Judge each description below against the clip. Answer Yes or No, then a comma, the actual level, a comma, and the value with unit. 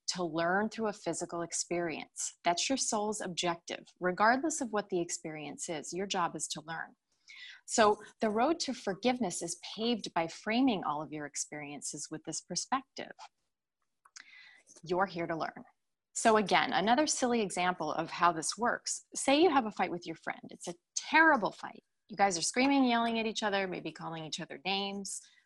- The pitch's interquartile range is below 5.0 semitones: No, wide, 5.5 semitones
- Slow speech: No, average, 175 wpm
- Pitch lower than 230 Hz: Yes, high, 190 Hz